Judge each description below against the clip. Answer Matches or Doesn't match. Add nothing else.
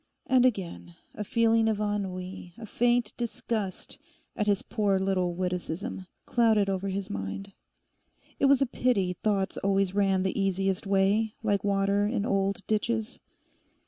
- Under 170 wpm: Matches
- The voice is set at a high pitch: Matches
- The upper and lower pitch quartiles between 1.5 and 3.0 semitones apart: Matches